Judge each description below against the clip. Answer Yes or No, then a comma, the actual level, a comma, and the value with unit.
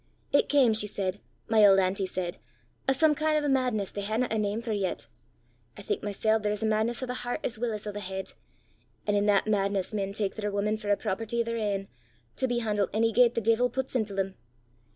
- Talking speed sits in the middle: No, fast, 235 wpm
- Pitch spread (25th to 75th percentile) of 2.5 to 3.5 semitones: Yes, average, 2.8 semitones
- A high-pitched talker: Yes, high, 215 Hz